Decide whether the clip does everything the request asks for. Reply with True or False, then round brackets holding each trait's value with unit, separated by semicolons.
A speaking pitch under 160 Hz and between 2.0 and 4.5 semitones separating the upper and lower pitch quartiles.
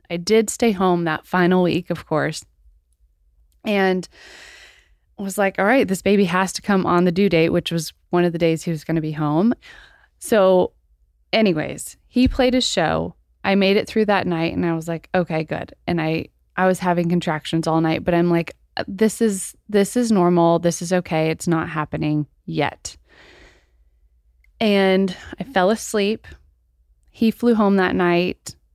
False (175 Hz; 4.0 semitones)